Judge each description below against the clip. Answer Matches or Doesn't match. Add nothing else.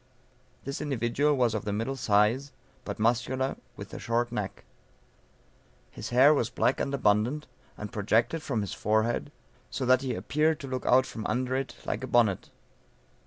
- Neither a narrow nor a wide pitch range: Matches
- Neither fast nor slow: Matches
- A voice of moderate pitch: Doesn't match